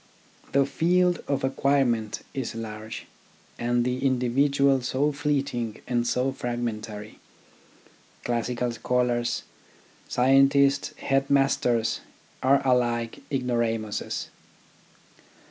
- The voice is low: Yes, low, 125 Hz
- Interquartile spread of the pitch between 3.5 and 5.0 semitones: No, narrow, 2.6 semitones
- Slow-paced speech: Yes, slow, 80 wpm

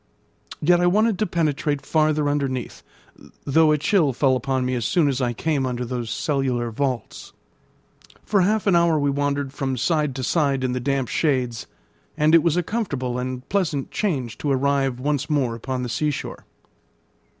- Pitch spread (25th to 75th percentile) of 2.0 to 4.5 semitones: Yes, average, 3.6 semitones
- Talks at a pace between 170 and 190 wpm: Yes, average, 180 wpm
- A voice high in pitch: No, medium, 140 Hz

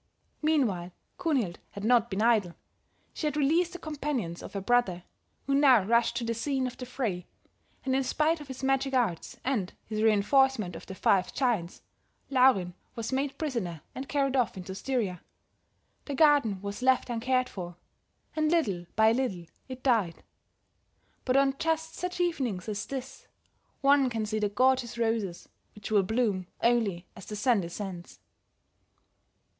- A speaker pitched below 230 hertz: No, high, 240 Hz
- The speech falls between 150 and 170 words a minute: Yes, average, 160 wpm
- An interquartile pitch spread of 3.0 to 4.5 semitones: No, average, 5.2 semitones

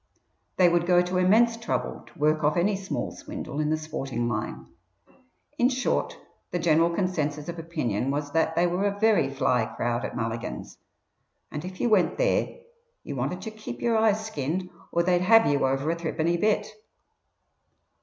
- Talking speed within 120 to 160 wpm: No, average, 175 wpm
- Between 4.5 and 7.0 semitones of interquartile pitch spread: Yes, average, 5.2 semitones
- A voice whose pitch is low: No, medium, 170 Hz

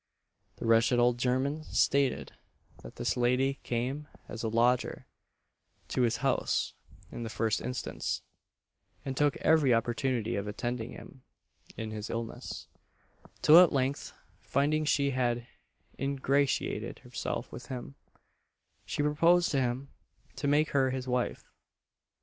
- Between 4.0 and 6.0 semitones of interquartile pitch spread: No, average, 2.8 semitones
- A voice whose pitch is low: Yes, low, 130 Hz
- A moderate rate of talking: No, slow, 130 wpm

